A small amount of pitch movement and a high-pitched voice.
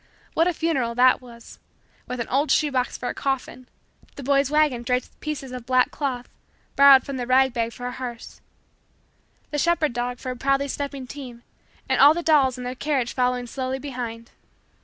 Yes: narrow, 2.2 semitones; very high, 255 Hz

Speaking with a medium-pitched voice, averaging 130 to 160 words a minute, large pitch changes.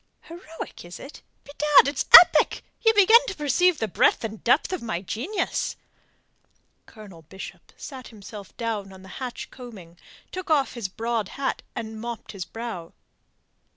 No: high, 235 Hz; average, 155 wpm; wide, 6.7 semitones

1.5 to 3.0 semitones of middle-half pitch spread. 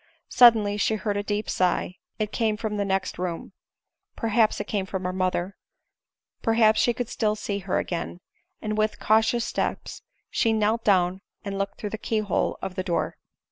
Yes: narrow, 2.4 semitones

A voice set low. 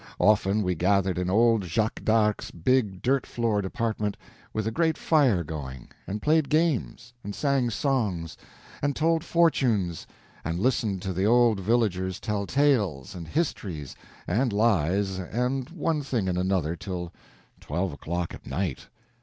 Yes: low, 105 Hz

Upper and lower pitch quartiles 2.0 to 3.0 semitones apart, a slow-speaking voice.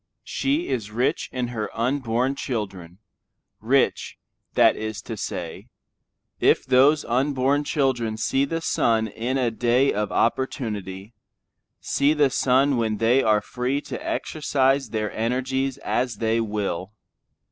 No: average, 3.6 semitones; slow, 130 wpm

